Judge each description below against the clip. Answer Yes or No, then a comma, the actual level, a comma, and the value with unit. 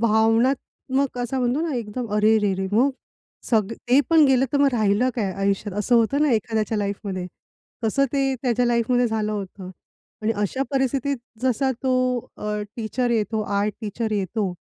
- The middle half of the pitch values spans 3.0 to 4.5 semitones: Yes, average, 3.6 semitones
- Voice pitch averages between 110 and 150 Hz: No, high, 225 Hz